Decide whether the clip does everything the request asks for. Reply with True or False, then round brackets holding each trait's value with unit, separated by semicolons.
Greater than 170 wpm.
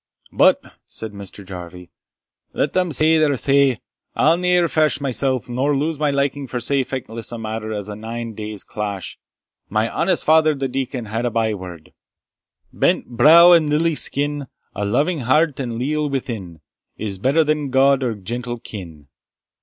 False (165 wpm)